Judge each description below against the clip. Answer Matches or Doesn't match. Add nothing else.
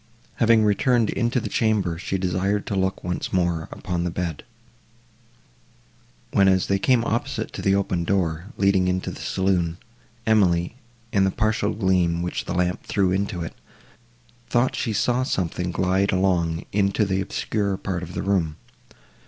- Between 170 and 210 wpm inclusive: Doesn't match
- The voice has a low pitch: Matches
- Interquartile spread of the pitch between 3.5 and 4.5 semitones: Doesn't match